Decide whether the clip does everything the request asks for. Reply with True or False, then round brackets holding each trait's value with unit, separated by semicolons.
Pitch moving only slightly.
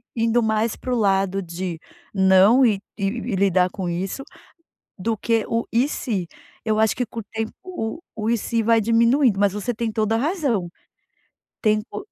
False (3.0 semitones)